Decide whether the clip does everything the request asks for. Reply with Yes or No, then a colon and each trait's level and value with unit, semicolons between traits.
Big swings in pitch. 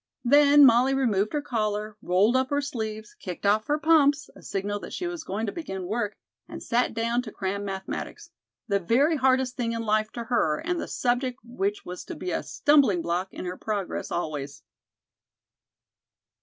No: average, 5.0 semitones